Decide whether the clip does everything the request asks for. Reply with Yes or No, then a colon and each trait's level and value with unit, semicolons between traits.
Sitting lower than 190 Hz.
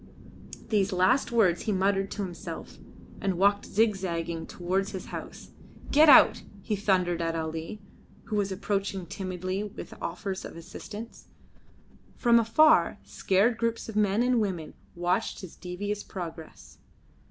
No: high, 195 Hz